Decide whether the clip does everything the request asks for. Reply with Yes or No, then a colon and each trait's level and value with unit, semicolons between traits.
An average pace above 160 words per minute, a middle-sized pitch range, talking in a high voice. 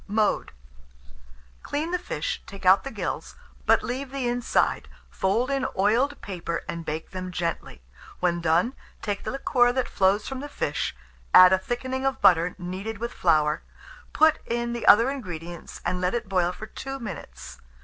No: average, 170 wpm; wide, 6.2 semitones; high, 210 Hz